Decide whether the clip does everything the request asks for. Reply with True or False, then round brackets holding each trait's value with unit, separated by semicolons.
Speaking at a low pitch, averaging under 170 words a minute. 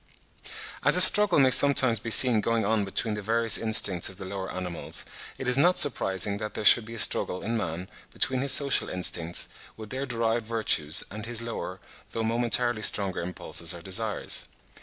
False (110 Hz; 185 wpm)